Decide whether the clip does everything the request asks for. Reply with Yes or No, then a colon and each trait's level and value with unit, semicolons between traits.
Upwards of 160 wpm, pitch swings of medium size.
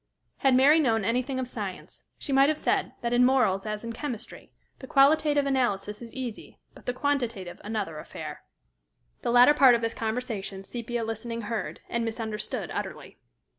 Yes: average, 170 wpm; average, 3.2 semitones